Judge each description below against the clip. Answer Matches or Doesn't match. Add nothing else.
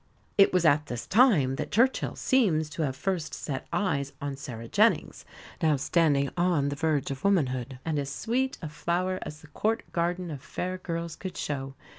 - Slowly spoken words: Doesn't match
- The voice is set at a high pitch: Doesn't match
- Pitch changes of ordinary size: Matches